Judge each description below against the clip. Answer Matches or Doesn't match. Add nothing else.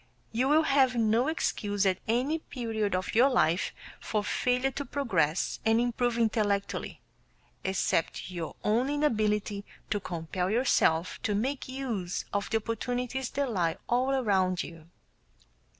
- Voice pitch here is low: Doesn't match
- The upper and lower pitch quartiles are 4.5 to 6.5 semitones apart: Matches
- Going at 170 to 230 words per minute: Doesn't match